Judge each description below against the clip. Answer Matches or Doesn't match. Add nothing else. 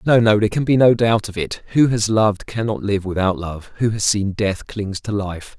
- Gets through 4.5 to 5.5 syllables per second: Matches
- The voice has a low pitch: Matches